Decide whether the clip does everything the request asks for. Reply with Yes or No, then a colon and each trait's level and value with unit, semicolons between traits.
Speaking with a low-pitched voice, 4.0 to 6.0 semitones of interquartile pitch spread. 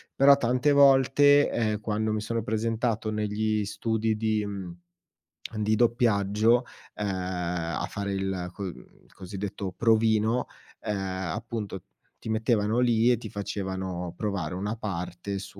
No: low, 105 Hz; average, 2.8 semitones